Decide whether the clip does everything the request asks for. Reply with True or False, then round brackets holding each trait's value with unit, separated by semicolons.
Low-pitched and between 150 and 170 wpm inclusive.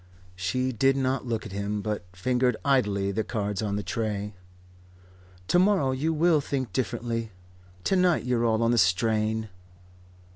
True (115 Hz; 155 wpm)